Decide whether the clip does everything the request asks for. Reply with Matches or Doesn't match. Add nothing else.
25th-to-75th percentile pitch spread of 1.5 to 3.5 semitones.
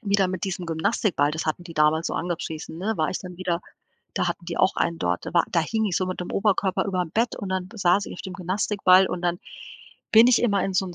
Matches